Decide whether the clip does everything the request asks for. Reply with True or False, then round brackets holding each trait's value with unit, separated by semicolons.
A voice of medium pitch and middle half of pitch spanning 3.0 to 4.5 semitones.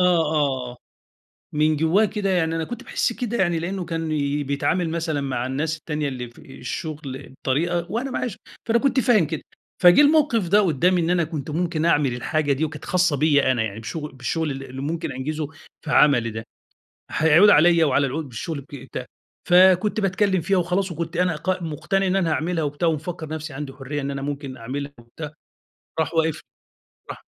True (160 Hz; 4.0 semitones)